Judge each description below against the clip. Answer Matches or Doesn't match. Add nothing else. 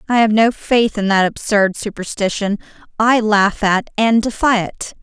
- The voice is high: Matches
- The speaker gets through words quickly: Doesn't match